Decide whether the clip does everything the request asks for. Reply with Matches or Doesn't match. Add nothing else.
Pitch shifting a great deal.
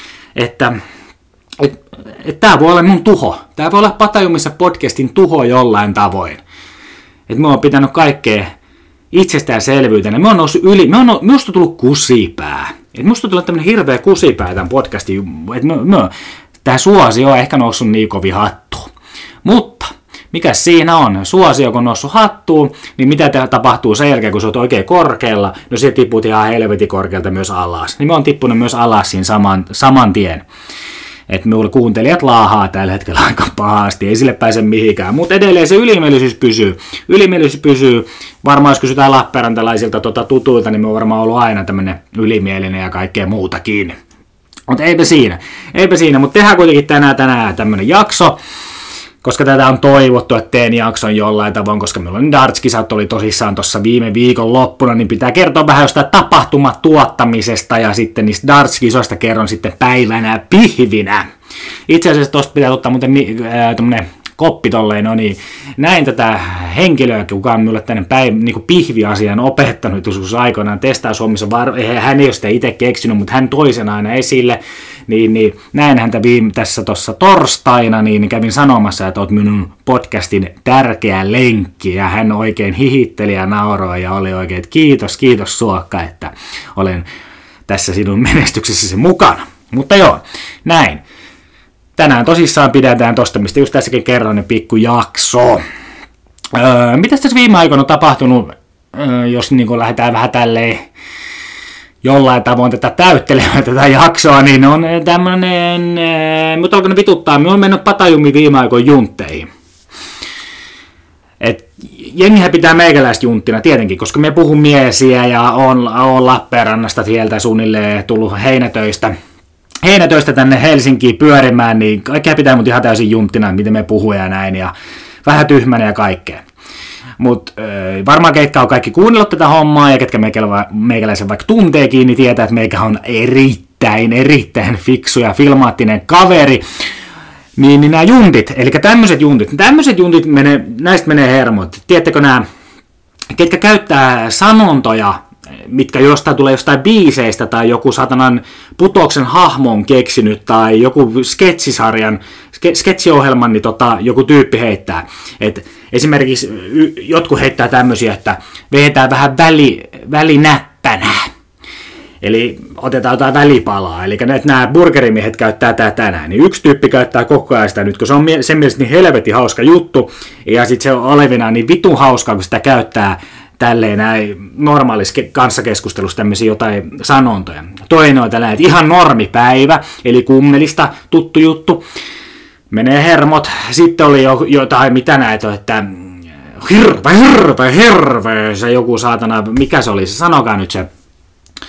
Doesn't match